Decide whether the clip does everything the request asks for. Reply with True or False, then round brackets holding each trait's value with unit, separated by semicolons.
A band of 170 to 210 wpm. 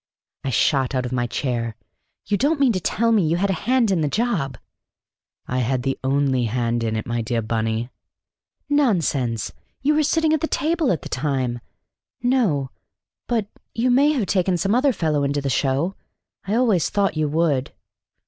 True (180 wpm)